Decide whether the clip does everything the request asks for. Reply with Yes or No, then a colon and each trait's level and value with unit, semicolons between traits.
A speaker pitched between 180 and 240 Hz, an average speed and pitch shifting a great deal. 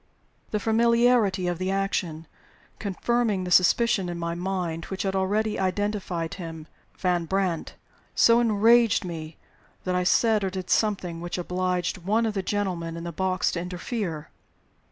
No: medium, 185 Hz; average, 155 wpm; average, 3.1 semitones